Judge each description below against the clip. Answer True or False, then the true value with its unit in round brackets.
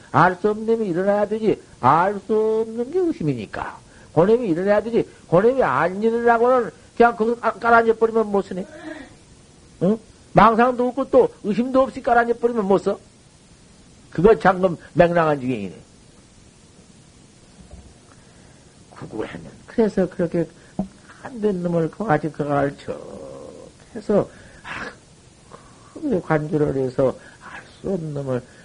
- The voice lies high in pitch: True (205 Hz)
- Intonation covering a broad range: True (6.0 semitones)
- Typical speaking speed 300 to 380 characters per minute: False (245 characters per minute)